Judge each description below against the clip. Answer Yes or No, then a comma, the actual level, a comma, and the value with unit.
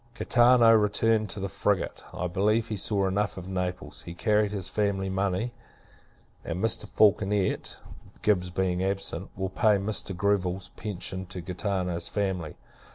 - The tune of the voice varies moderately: No, narrow, 2.3 semitones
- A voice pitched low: Yes, very low, 95 Hz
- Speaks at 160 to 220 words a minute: No, average, 145 wpm